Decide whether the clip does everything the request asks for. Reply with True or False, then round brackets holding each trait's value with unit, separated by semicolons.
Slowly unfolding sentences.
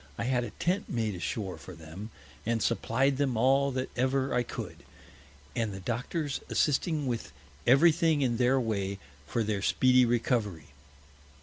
False (160 wpm)